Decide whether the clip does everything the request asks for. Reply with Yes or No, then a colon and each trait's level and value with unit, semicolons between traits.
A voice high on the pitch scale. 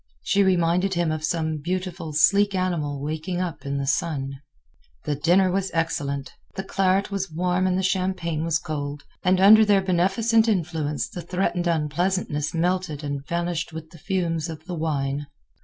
No: medium, 170 Hz